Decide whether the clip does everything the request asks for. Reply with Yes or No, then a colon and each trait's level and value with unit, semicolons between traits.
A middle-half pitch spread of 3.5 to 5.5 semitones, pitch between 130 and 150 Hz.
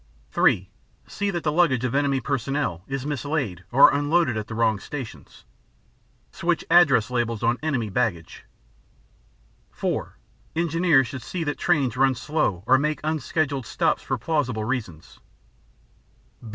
Yes: average, 4.9 semitones; low, 135 Hz